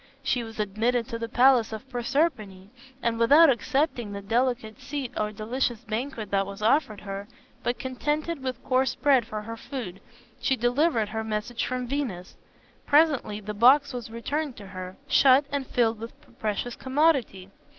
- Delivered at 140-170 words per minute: Yes, average, 165 wpm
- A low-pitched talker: No, high, 240 Hz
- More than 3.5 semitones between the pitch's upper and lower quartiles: Yes, average, 3.9 semitones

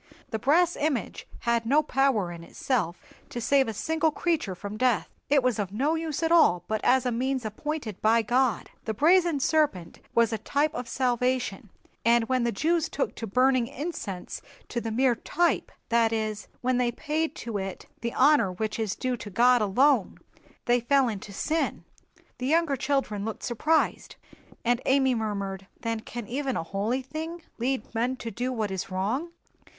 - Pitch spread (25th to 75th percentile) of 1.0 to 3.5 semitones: No, average, 4.4 semitones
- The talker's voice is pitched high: Yes, high, 245 Hz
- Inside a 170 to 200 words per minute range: Yes, average, 180 wpm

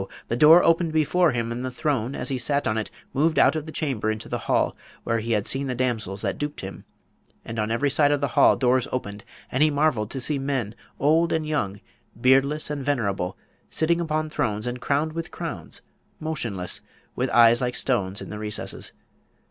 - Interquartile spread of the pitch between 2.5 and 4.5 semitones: No, average, 5.1 semitones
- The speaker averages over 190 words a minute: Yes, fast, 205 wpm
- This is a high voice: No, low, 130 Hz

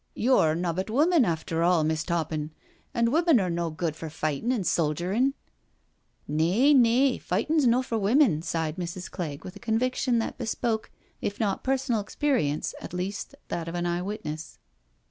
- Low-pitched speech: No, medium, 185 Hz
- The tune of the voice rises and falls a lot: Yes, wide, 6.7 semitones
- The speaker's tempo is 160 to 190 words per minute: Yes, average, 170 wpm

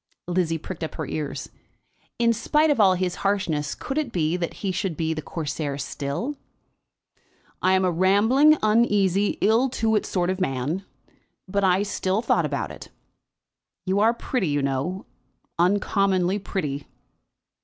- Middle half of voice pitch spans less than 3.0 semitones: No, average, 4.3 semitones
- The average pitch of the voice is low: No, medium, 185 Hz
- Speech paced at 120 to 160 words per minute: Yes, average, 155 wpm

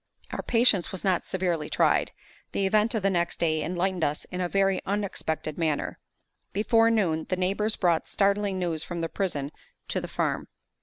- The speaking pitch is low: No, medium, 185 Hz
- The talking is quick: No, average, 175 wpm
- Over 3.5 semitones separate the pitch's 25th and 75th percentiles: No, average, 3.1 semitones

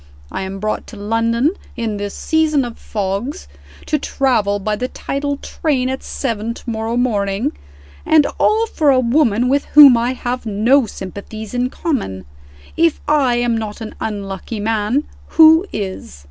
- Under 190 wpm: Yes, average, 160 wpm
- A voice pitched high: Yes, high, 235 Hz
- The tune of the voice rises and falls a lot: No, average, 4.8 semitones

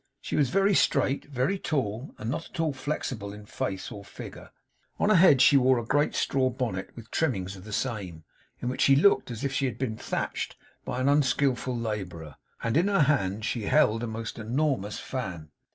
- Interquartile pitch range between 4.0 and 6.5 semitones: Yes, average, 4.9 semitones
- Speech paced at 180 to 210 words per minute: Yes, average, 200 wpm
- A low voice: Yes, low, 125 Hz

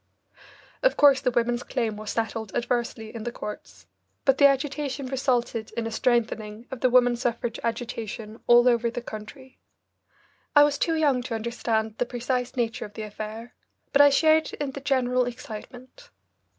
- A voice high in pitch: Yes, high, 240 Hz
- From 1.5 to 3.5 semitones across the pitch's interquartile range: Yes, average, 2.7 semitones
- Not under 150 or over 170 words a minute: Yes, average, 165 wpm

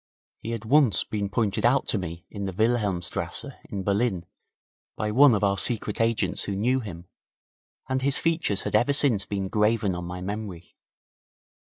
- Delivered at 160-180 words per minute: Yes, average, 170 wpm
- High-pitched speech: No, low, 105 Hz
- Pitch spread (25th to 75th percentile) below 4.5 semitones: Yes, average, 3.5 semitones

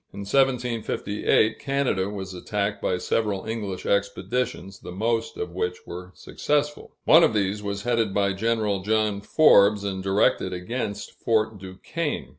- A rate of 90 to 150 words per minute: Yes, average, 140 wpm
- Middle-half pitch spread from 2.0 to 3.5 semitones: Yes, average, 2.9 semitones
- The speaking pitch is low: Yes, low, 105 Hz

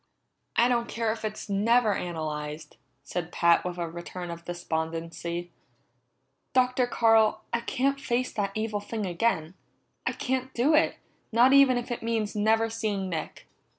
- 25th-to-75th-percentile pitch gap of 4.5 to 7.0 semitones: Yes, wide, 5.4 semitones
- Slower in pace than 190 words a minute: Yes, average, 150 wpm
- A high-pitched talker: Yes, high, 215 Hz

